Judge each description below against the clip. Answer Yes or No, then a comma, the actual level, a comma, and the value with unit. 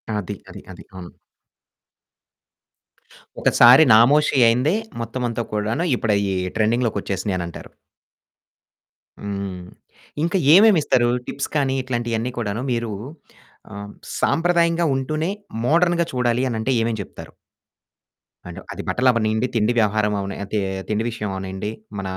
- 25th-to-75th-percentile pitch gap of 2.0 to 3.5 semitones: No, average, 3.9 semitones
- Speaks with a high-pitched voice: No, low, 115 Hz